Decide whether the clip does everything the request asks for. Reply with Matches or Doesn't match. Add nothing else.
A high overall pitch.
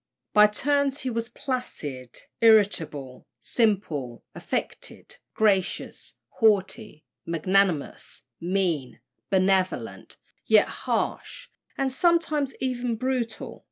Matches